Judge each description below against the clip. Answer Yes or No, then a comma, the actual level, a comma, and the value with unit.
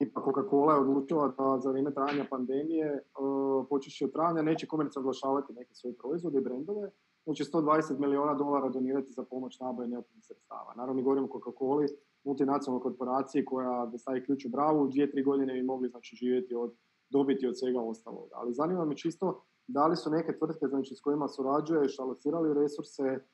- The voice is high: No, low, 135 Hz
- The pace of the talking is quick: Yes, fast, 190 wpm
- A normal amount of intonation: No, narrow, 2.0 semitones